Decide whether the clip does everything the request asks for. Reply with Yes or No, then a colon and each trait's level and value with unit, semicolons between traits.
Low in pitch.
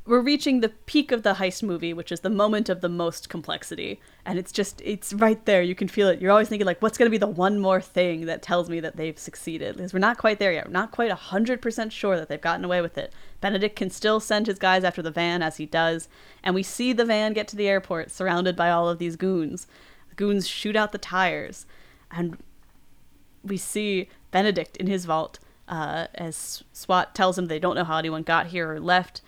No: medium, 185 Hz